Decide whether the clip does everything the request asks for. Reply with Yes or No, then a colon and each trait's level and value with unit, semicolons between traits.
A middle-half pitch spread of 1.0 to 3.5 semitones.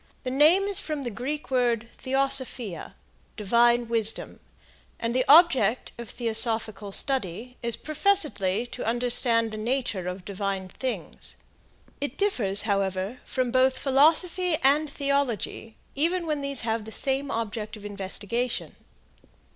No: average, 4.3 semitones